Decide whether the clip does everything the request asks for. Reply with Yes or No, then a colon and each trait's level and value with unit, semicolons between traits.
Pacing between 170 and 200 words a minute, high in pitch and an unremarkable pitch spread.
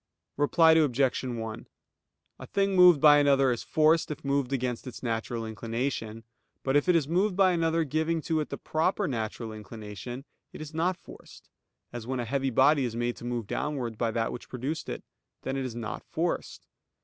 No: average, 190 wpm; low, 135 Hz; average, 5.0 semitones